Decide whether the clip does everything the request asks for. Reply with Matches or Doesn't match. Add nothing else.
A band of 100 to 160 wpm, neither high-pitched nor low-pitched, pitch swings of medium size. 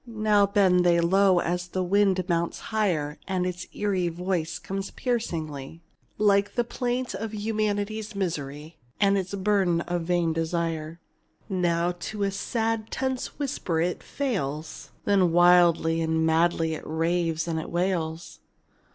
Matches